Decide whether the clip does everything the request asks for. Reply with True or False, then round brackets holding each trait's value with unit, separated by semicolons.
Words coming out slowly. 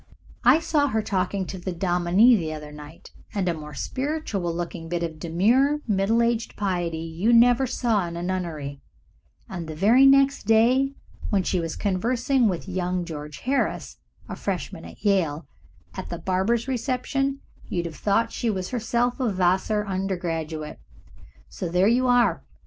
False (160 wpm)